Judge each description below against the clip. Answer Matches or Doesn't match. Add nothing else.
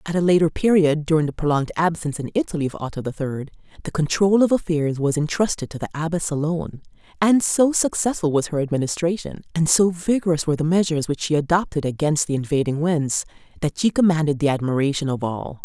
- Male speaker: Doesn't match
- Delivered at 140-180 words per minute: Doesn't match